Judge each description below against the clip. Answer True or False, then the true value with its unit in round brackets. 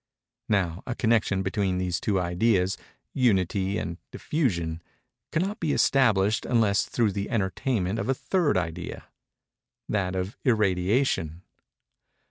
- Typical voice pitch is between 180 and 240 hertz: False (100 Hz)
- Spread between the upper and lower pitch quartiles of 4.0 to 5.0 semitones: True (4.4 semitones)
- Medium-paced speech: False (100 wpm)